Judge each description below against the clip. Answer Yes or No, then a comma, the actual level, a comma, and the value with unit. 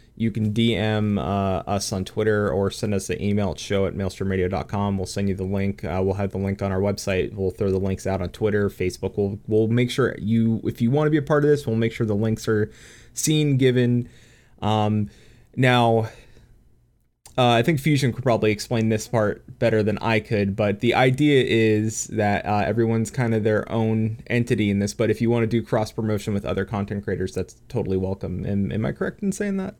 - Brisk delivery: Yes, fast, 220 wpm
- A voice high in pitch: No, low, 110 Hz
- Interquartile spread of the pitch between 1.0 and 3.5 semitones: Yes, average, 2.8 semitones